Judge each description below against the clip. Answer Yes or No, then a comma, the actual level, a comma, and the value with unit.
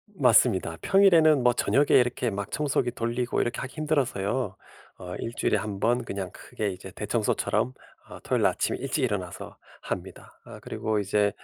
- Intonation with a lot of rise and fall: No, average, 4.9 semitones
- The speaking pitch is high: No, low, 120 Hz